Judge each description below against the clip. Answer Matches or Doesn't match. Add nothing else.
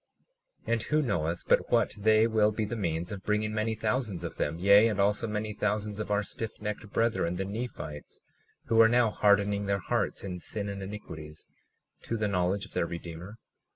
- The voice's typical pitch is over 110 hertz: Doesn't match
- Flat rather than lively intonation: Matches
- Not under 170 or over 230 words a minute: Matches